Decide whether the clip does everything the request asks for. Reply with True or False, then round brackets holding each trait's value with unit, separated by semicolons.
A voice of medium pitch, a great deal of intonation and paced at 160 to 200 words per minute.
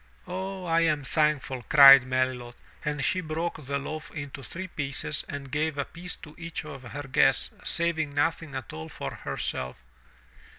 False (145 Hz; 3.3 semitones; 165 wpm)